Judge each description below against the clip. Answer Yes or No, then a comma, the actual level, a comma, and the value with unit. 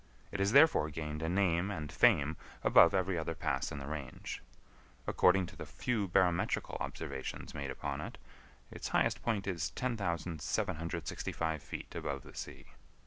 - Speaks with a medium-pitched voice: No, very low, 85 Hz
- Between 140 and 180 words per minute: Yes, average, 150 wpm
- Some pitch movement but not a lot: Yes, average, 4.3 semitones